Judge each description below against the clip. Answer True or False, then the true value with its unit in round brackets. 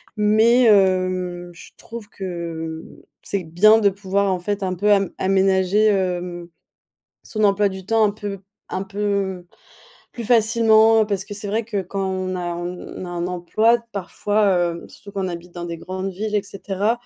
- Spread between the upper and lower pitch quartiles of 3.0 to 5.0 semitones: False (2.5 semitones)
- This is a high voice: True (195 Hz)